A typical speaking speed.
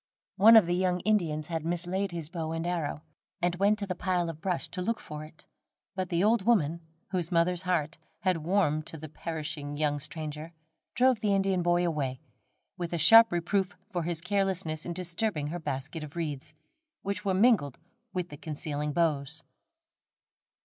Yes: average, 175 wpm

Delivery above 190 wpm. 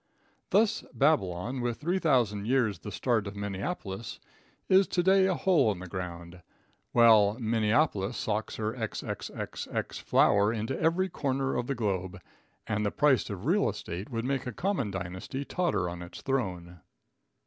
No: average, 150 wpm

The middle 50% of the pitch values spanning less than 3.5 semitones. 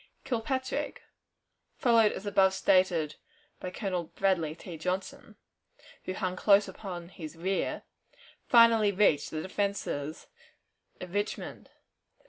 Yes: average, 3.0 semitones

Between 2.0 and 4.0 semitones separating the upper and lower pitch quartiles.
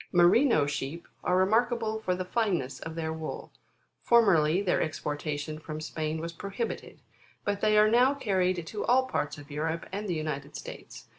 No: wide, 5.5 semitones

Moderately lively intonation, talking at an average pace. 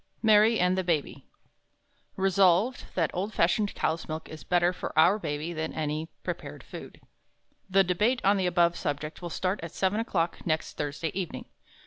Yes: average, 3.4 semitones; average, 170 wpm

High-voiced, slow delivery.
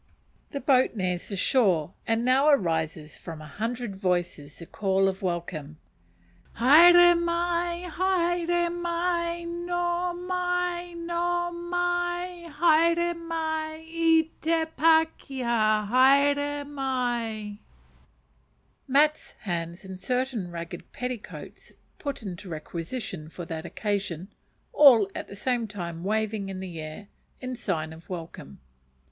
Yes: very high, 255 Hz; slow, 120 wpm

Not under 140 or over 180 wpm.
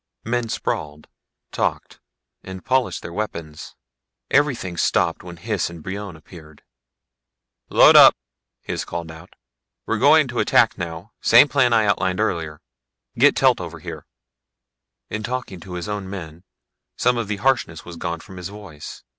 Yes: average, 150 wpm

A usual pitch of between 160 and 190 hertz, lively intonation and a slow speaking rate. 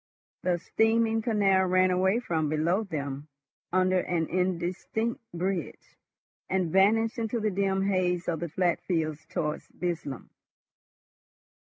No: medium, 185 Hz; average, 2.9 semitones; slow, 120 wpm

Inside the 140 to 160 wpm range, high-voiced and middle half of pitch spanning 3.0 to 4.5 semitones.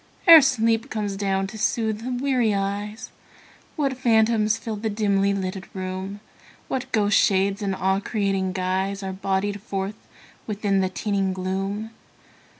No: average, 145 wpm; high, 205 Hz; narrow, 2.4 semitones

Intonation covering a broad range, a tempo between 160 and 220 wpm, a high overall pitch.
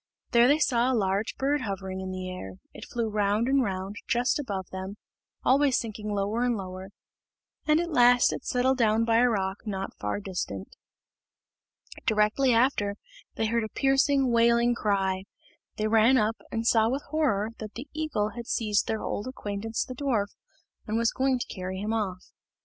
No: average, 3.7 semitones; average, 180 wpm; high, 225 Hz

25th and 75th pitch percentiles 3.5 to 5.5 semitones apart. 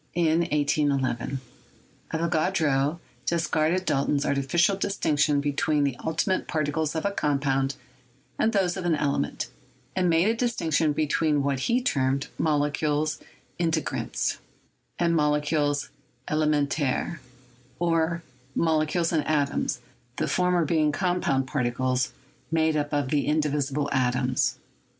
No: average, 2.8 semitones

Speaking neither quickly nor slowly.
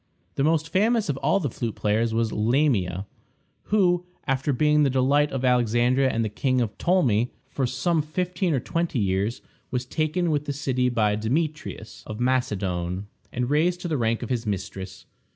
Yes: average, 170 wpm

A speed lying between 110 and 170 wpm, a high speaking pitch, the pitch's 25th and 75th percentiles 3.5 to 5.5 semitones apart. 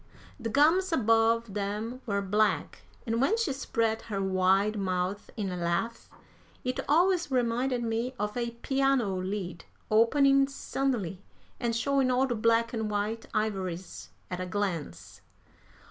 Yes: average, 140 wpm; high, 225 Hz; average, 4.4 semitones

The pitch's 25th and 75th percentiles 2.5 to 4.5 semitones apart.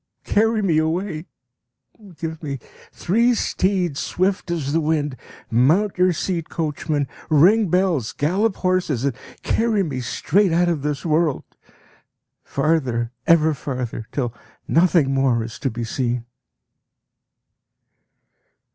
No: average, 5.1 semitones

